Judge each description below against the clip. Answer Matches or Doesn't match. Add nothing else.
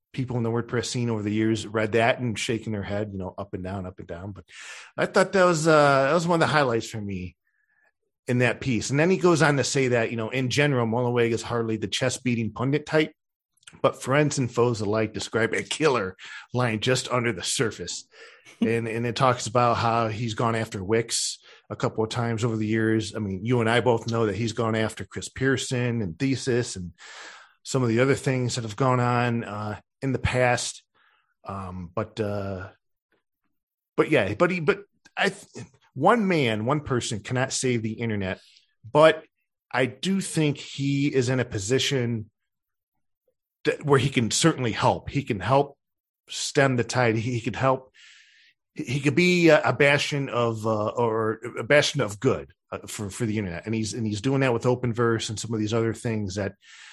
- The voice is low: Matches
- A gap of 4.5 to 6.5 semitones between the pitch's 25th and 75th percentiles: Doesn't match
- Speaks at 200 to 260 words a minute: Matches